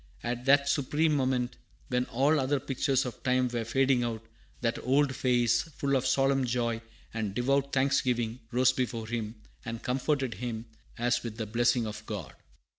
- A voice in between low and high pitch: No, low, 125 Hz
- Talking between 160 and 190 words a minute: Yes, average, 165 wpm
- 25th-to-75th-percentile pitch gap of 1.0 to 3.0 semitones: Yes, narrow, 2.5 semitones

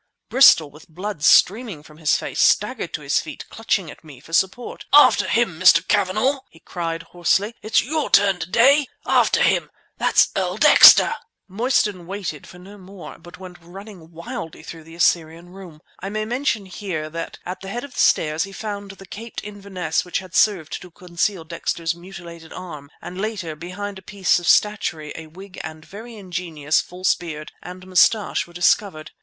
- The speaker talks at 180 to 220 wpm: Yes, average, 185 wpm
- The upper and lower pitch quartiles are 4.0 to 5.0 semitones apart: No, average, 3.6 semitones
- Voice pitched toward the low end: No, medium, 185 Hz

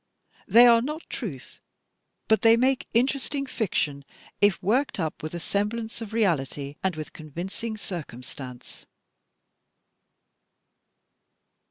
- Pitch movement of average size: No, wide, 7.0 semitones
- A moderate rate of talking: No, slow, 110 wpm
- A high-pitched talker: Yes, high, 205 Hz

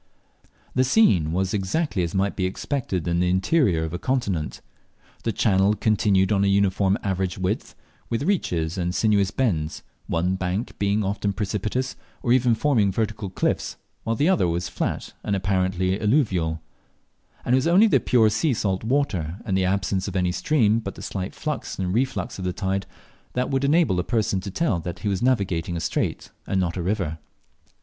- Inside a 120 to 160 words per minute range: No, average, 185 wpm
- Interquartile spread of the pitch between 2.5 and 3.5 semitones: No, average, 3.9 semitones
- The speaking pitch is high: No, low, 100 Hz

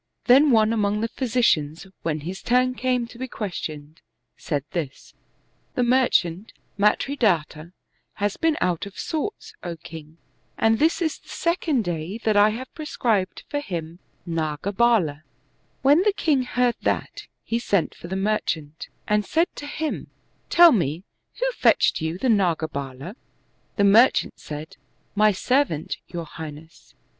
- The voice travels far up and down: Yes, wide, 7.6 semitones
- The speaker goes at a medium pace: Yes, average, 150 wpm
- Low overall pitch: No, high, 205 Hz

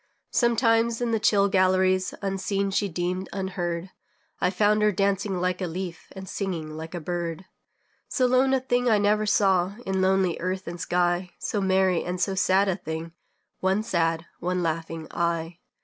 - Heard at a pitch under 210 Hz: Yes, high, 190 Hz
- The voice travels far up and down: No, narrow, 2.4 semitones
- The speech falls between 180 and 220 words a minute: No, average, 170 wpm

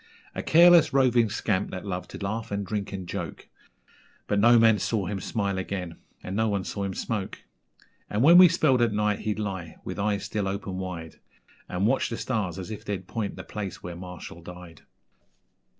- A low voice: Yes, low, 100 Hz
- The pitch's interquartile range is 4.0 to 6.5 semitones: No, average, 3.2 semitones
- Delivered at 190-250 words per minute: Yes, average, 195 wpm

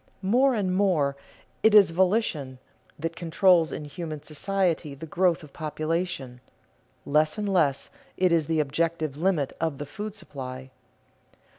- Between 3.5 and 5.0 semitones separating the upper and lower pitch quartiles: Yes, average, 4.1 semitones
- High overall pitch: No, medium, 165 Hz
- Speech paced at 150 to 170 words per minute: No, average, 140 wpm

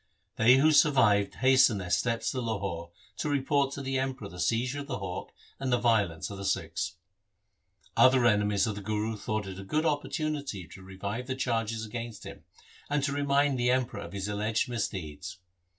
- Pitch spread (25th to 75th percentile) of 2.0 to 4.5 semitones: No, average, 4.9 semitones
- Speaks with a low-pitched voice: Yes, low, 115 Hz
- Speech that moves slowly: No, average, 190 wpm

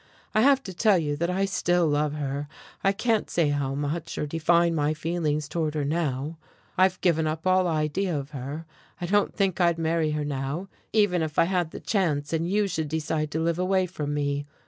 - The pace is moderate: No, fast, 210 wpm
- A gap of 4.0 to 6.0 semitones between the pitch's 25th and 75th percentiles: No, average, 3.6 semitones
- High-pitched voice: No, medium, 160 Hz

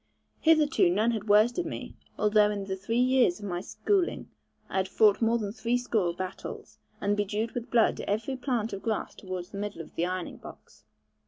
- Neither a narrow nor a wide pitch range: Yes, average, 3.4 semitones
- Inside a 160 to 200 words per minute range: Yes, average, 185 wpm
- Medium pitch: No, high, 210 Hz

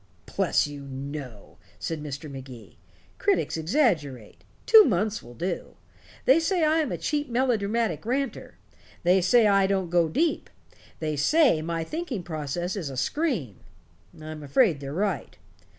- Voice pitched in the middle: Yes, medium, 175 Hz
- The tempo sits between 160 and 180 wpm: No, average, 145 wpm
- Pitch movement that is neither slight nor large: No, wide, 8.9 semitones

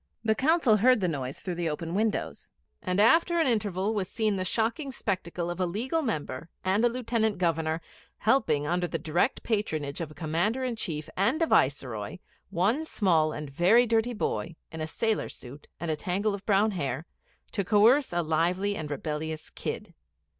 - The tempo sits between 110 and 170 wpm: No, average, 180 wpm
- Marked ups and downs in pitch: Yes, wide, 5.7 semitones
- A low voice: No, medium, 185 Hz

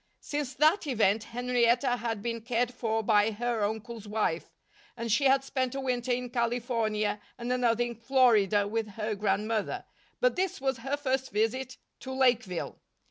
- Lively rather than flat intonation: No, average, 2.8 semitones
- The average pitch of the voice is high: Yes, high, 235 Hz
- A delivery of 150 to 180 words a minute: Yes, average, 160 wpm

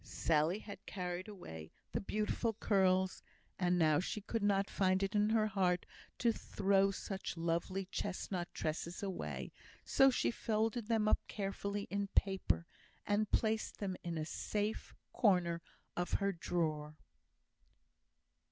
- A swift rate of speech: No, slow, 135 wpm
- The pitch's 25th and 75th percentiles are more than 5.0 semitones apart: No, average, 2.9 semitones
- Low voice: No, high, 195 Hz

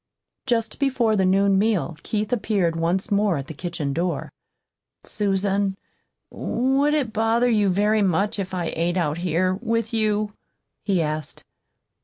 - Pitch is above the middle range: Yes, high, 200 Hz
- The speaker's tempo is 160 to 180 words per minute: No, average, 145 wpm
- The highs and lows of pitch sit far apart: No, average, 3.7 semitones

